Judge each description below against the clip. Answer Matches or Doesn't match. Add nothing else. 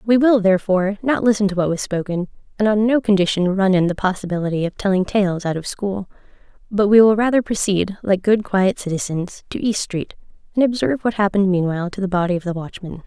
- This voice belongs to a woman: Matches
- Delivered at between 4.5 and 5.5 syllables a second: Doesn't match